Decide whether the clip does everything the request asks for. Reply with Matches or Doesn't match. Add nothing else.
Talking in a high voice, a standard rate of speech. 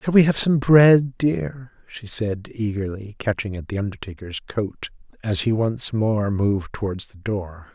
Doesn't match